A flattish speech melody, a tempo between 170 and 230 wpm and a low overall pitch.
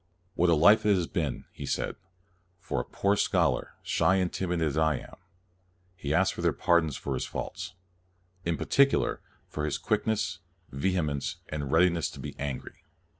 No: average, 3.4 semitones; average, 180 wpm; very low, 85 Hz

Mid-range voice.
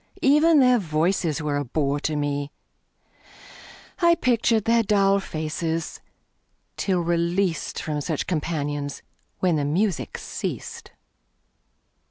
Yes: medium, 170 Hz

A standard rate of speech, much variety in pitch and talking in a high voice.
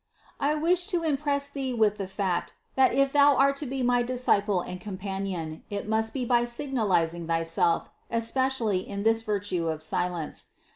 Yes: average, 165 wpm; wide, 6.3 semitones; high, 225 Hz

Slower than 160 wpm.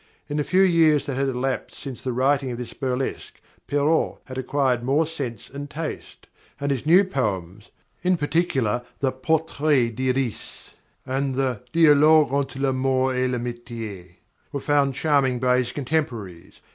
Yes: average, 150 wpm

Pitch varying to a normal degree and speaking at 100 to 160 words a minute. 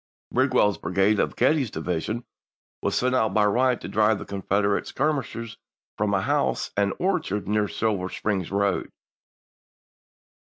Yes: average, 3.8 semitones; average, 145 wpm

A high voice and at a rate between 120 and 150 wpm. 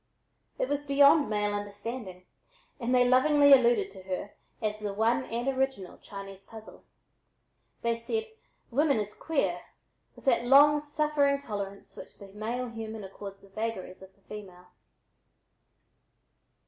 Yes: high, 225 Hz; slow, 135 wpm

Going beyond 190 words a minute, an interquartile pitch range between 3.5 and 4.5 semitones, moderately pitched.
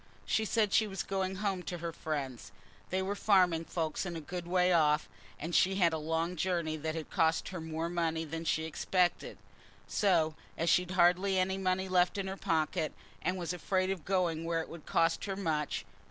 No: average, 200 wpm; average, 2.7 semitones; medium, 175 Hz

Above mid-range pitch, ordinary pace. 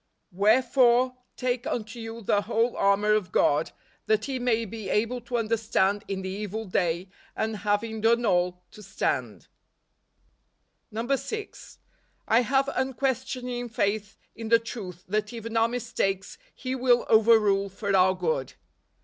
Yes: high, 220 Hz; average, 150 wpm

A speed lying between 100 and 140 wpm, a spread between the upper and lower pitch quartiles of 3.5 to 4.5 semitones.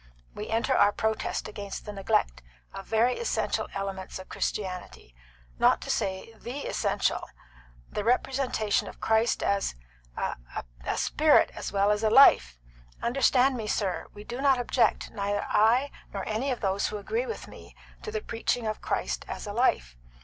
No: average, 165 wpm; average, 3.9 semitones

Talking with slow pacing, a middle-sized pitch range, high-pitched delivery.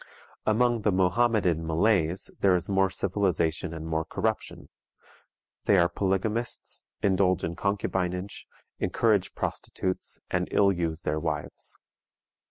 No: slow, 115 wpm; average, 3.2 semitones; very low, 95 Hz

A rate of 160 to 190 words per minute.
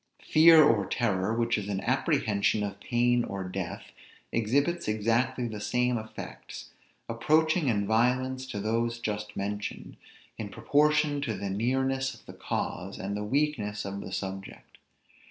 No: average, 145 wpm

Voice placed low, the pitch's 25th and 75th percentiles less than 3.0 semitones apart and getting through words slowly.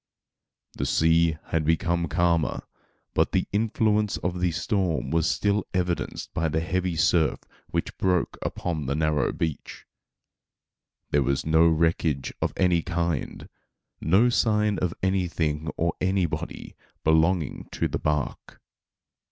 Yes: very low, 85 Hz; narrow, 2.5 semitones; slow, 125 wpm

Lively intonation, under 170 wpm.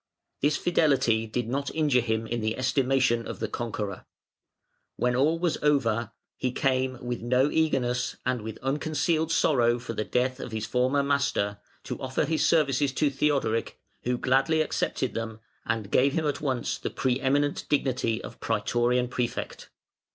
No: average, 3.2 semitones; average, 160 wpm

